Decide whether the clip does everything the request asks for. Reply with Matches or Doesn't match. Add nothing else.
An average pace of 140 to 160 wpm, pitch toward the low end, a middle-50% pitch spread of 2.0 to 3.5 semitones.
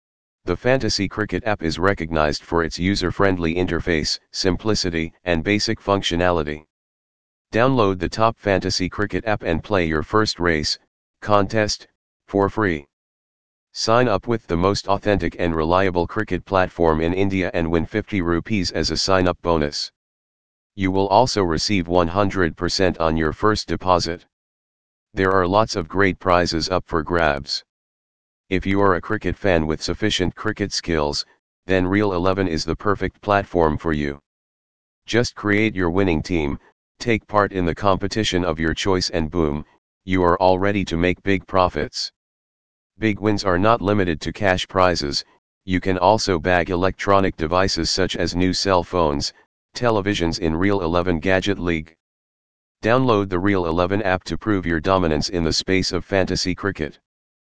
Matches